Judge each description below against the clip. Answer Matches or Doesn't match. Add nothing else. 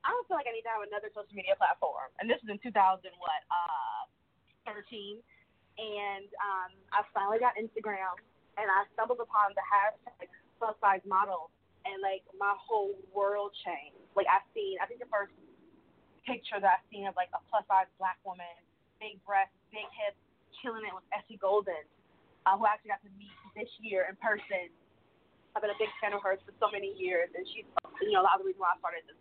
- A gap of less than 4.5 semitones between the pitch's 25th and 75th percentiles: Matches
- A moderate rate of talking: Doesn't match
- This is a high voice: Matches